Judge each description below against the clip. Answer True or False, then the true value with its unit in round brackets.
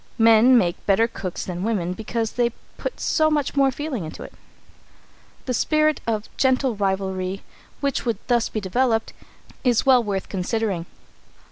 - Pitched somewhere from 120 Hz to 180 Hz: False (225 Hz)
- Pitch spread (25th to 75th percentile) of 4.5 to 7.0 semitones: True (4.8 semitones)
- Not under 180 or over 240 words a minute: False (150 wpm)